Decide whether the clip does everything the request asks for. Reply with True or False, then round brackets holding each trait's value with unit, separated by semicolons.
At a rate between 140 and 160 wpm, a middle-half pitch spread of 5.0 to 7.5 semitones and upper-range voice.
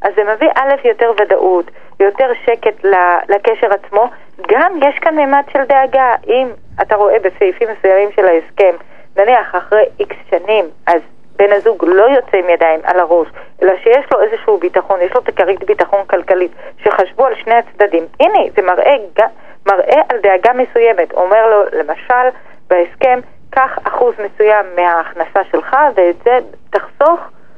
True (150 wpm; 5.6 semitones; 220 Hz)